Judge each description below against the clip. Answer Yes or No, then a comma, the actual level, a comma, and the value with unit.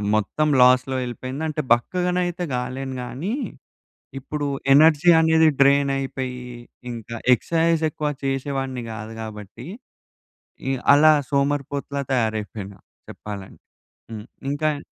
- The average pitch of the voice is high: No, low, 135 Hz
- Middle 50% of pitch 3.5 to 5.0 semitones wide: Yes, average, 3.9 semitones